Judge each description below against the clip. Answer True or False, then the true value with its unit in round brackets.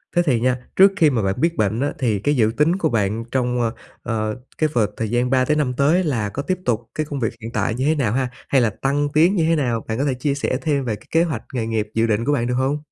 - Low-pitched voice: True (125 Hz)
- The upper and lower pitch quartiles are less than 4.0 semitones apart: False (4.5 semitones)